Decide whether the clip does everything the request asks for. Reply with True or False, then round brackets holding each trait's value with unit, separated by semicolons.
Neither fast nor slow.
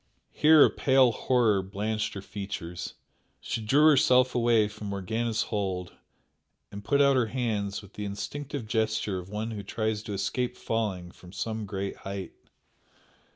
True (155 wpm)